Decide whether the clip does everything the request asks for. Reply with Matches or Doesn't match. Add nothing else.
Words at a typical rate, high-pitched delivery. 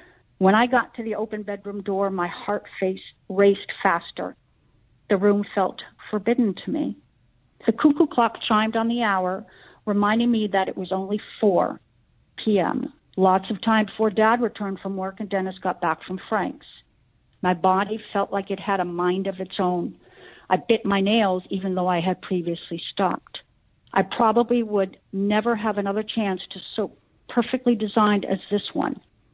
Matches